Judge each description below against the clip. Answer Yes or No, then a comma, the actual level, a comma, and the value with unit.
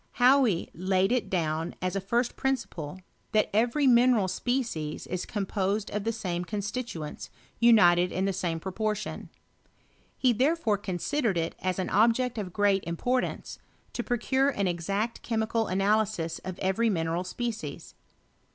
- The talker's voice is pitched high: Yes, high, 205 Hz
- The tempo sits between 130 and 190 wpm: Yes, average, 145 wpm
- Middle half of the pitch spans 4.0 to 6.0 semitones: Yes, average, 4.5 semitones